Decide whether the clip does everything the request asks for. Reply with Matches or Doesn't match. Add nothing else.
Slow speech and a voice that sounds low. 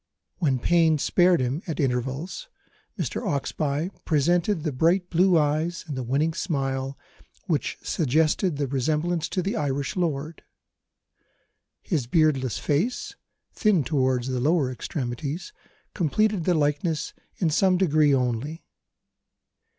Doesn't match